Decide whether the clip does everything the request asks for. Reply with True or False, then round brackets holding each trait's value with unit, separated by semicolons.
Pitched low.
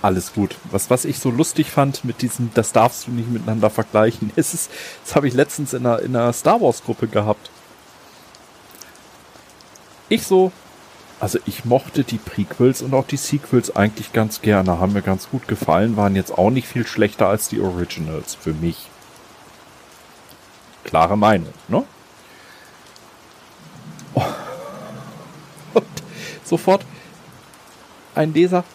True (120 Hz)